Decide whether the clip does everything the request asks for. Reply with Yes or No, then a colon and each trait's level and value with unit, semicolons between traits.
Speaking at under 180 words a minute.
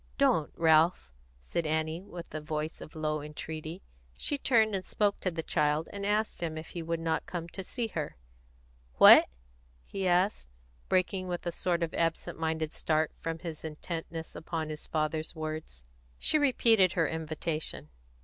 Yes: average, 165 wpm